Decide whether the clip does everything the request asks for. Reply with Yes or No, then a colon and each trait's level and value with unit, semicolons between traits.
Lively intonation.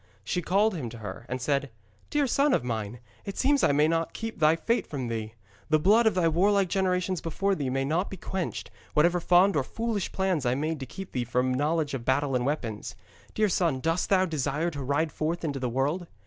Yes: wide, 5.8 semitones